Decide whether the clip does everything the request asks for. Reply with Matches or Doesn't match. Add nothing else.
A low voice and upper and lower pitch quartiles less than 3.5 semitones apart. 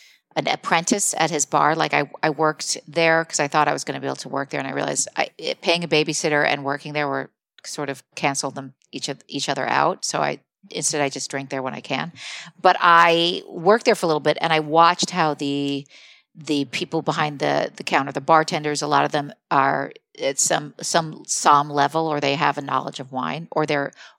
Doesn't match